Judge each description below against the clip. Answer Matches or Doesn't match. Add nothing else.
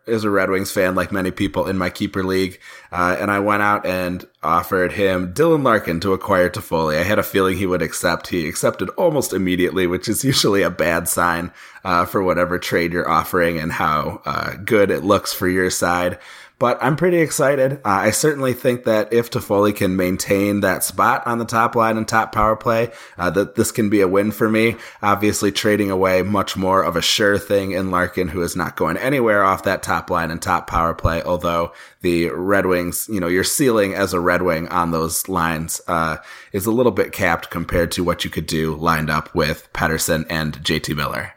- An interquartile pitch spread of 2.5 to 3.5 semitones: Matches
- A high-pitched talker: Doesn't match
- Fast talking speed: Matches